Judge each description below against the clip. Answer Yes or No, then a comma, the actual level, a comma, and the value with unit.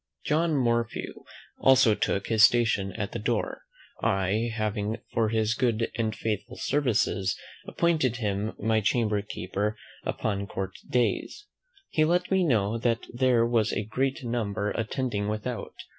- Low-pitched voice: Yes, low, 115 Hz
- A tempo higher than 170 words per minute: No, average, 140 wpm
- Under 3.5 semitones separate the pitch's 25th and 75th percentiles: Yes, average, 2.8 semitones